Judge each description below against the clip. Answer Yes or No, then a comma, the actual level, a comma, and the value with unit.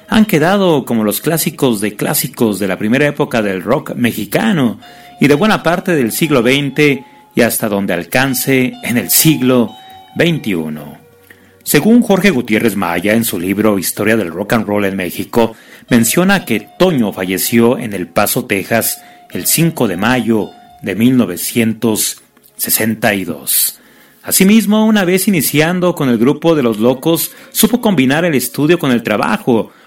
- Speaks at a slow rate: No, average, 150 wpm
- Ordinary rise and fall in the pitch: No, wide, 7.3 semitones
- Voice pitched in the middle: No, low, 130 Hz